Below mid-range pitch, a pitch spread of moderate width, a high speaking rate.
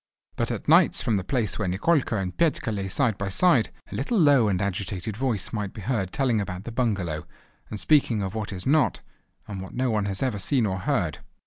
Yes: low, 105 Hz; average, 4.7 semitones; fast, 220 wpm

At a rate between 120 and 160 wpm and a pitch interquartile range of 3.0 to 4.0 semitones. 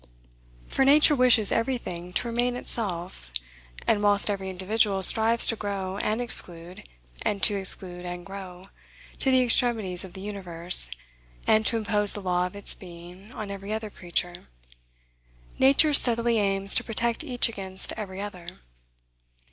Yes: average, 150 wpm; average, 3.7 semitones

